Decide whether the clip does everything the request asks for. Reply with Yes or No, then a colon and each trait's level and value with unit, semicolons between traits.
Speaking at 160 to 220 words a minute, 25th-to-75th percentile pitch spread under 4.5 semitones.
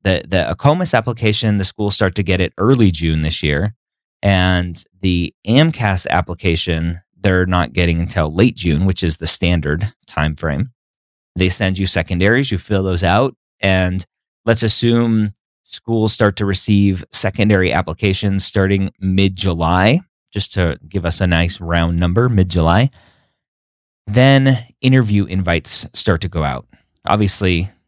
No: average, 145 wpm; average, 3.5 semitones